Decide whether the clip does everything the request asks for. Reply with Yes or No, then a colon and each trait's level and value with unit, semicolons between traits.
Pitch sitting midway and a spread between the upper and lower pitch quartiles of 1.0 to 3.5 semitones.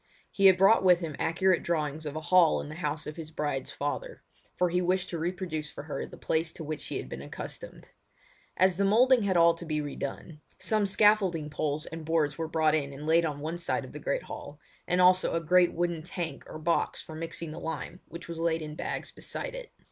Yes: medium, 165 Hz; average, 2.8 semitones